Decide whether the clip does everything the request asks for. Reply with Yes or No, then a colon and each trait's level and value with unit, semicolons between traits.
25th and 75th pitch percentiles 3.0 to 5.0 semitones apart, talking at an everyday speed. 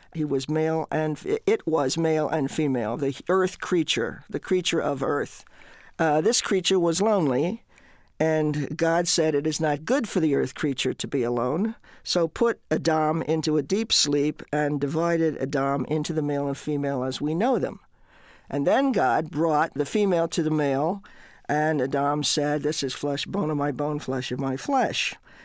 No: narrow, 2.6 semitones; average, 180 wpm